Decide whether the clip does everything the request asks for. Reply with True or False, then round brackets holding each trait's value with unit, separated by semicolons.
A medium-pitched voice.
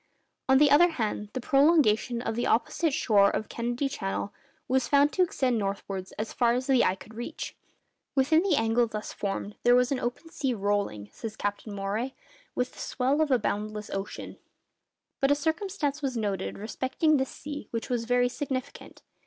False (245 Hz)